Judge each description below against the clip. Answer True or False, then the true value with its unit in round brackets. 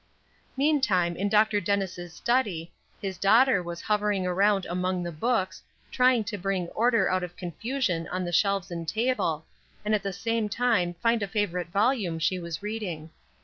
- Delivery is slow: False (165 wpm)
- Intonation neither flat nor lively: True (4.0 semitones)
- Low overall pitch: False (195 Hz)